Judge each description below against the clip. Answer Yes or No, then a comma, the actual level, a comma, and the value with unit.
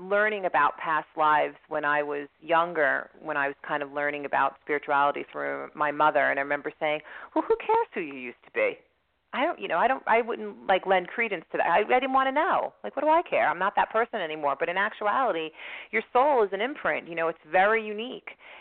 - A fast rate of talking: Yes, fast, 235 wpm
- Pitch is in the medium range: Yes, medium, 170 Hz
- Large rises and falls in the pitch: Yes, wide, 7.3 semitones